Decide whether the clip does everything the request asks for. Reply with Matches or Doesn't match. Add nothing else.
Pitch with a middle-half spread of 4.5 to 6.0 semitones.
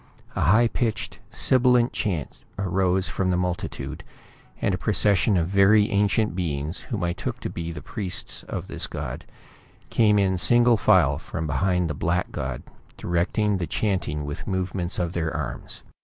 Doesn't match